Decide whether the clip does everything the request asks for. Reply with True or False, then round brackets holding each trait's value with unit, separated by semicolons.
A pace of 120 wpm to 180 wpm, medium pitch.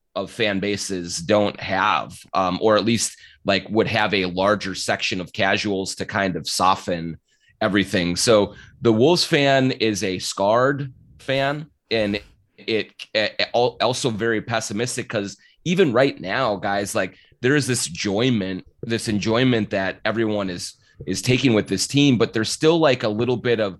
False (165 wpm; 110 Hz)